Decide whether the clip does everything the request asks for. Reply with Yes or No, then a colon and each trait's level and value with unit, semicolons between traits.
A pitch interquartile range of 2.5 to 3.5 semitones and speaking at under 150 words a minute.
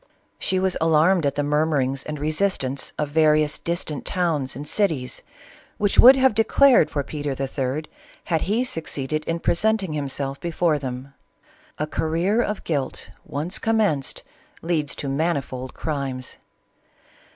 No: average, 4.2 semitones; average, 140 wpm